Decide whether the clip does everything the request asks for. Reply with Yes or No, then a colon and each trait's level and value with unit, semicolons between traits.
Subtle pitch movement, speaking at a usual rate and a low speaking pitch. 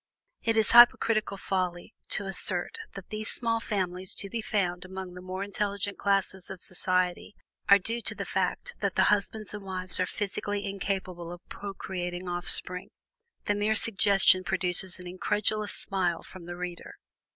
No: narrow, 2.2 semitones; average, 160 wpm; high, 195 Hz